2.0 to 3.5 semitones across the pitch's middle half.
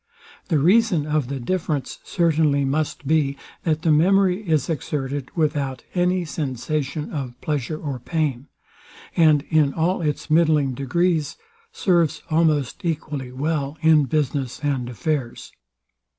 Yes: average, 2.8 semitones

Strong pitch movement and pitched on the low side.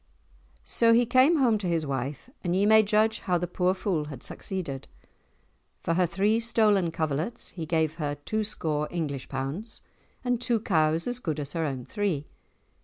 No: wide, 6.1 semitones; medium, 175 Hz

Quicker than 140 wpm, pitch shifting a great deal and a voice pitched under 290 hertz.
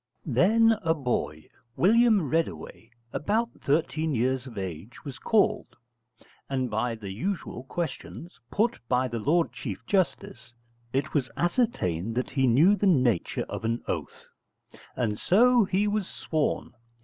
No: slow, 135 wpm; wide, 8.5 semitones; medium, 140 Hz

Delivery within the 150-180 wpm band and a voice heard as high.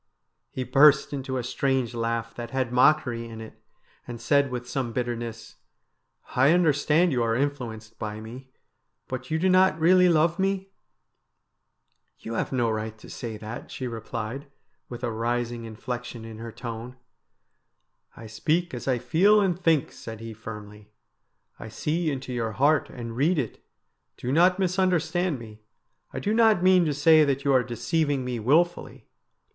No: average, 175 wpm; low, 130 Hz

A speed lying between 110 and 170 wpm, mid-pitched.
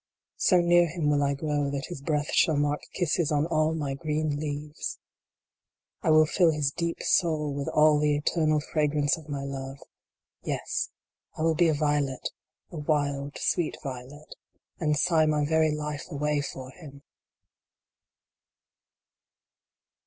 Yes: average, 145 wpm; medium, 150 Hz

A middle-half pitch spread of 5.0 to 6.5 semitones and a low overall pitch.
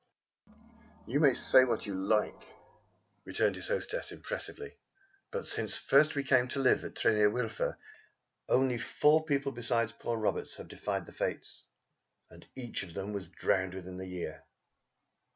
Yes: wide, 5.6 semitones; low, 120 Hz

